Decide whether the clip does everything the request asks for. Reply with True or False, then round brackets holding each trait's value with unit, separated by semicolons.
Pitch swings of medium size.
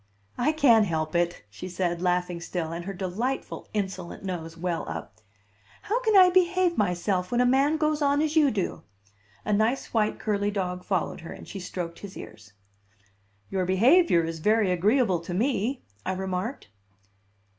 False (6.5 semitones)